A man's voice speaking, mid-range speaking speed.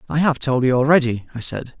No: male; fast, 235 wpm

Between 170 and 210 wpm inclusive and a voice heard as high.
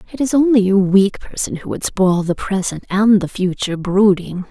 Yes: average, 200 wpm; high, 195 Hz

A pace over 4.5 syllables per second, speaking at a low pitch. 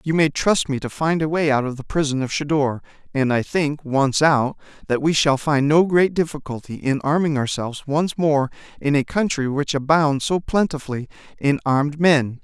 No: 5.0 syllables/s; medium, 145 Hz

